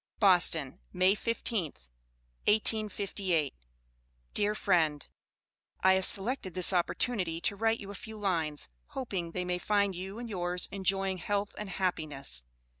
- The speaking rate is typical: No, slow, 130 wpm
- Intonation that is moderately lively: Yes, average, 3.0 semitones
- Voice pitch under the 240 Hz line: Yes, high, 190 Hz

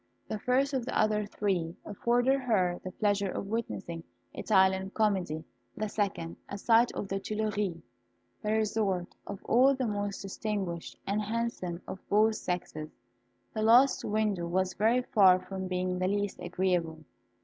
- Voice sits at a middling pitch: No, high, 200 Hz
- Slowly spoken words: No, average, 150 wpm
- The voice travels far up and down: No, average, 2.9 semitones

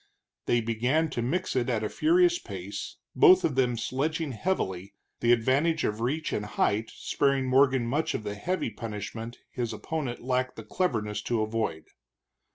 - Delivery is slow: No, average, 165 wpm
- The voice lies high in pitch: No, low, 125 Hz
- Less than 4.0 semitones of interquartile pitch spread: No, wide, 5.5 semitones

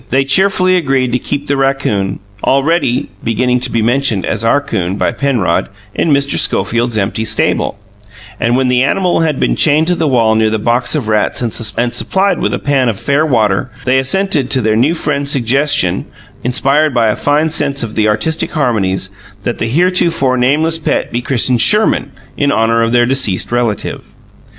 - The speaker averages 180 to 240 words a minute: Yes, average, 185 wpm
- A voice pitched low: Yes, low, 130 Hz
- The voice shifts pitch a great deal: No, average, 3.9 semitones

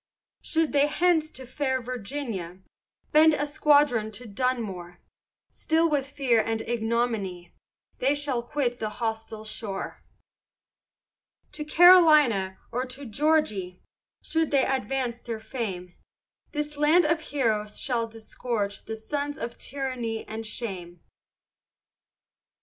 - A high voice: Yes, high, 245 Hz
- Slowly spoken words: Yes, slow, 120 wpm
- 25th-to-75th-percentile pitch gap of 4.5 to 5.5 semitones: Yes, average, 5.0 semitones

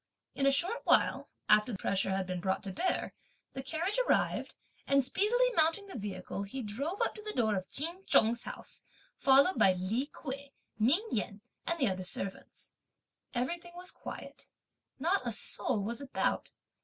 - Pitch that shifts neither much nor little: No, wide, 8.8 semitones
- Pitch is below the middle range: No, very high, 265 Hz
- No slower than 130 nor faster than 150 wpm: No, average, 165 wpm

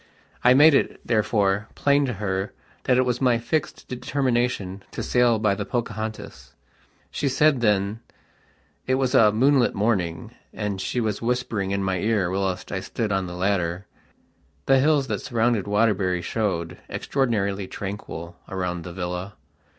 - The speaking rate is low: No, average, 150 wpm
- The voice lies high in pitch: No, low, 105 Hz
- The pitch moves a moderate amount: Yes, average, 4.4 semitones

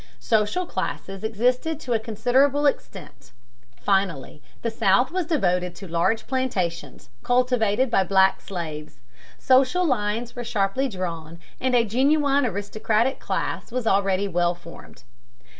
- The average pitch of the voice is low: No, high, 220 Hz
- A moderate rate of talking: No, slow, 125 wpm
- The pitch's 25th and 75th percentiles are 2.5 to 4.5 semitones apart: No, average, 5.2 semitones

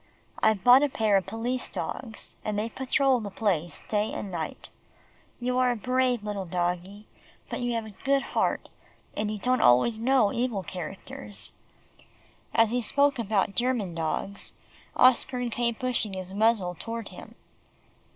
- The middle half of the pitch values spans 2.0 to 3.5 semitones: No, average, 4.1 semitones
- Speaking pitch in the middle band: No, high, 220 Hz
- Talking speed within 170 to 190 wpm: No, average, 155 wpm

